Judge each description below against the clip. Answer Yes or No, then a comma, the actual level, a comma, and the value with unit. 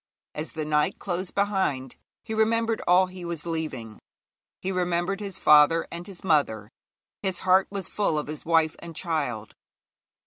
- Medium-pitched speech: Yes, medium, 170 Hz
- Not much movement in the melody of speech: No, average, 3.9 semitones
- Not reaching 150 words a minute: No, average, 160 wpm